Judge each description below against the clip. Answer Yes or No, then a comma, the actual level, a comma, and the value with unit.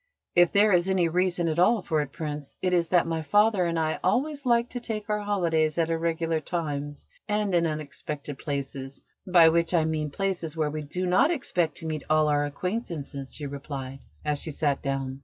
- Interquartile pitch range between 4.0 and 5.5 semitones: No, average, 3.6 semitones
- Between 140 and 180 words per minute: No, average, 200 wpm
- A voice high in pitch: No, medium, 165 Hz